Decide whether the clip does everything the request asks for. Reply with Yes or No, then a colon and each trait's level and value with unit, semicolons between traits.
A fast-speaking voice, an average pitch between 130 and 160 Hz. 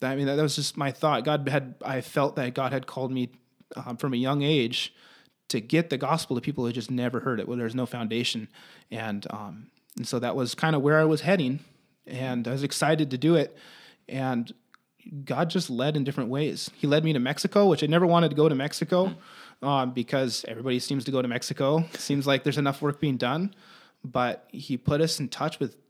Yes: fast, 225 wpm; medium, 140 Hz